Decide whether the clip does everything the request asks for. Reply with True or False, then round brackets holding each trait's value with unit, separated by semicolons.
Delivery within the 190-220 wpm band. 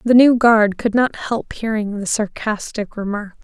False (175 wpm)